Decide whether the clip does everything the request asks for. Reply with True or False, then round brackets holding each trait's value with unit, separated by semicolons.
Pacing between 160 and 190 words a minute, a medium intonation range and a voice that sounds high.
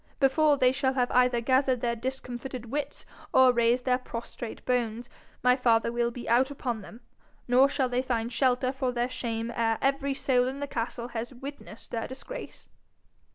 False (175 wpm; 1.9 semitones; 250 Hz)